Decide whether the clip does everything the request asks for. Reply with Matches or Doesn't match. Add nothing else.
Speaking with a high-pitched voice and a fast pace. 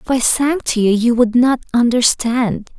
Doesn't match